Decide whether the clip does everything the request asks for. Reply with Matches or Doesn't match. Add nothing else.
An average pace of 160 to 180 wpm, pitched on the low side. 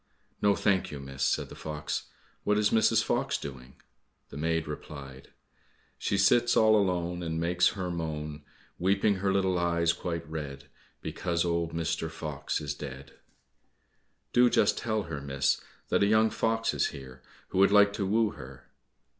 Matches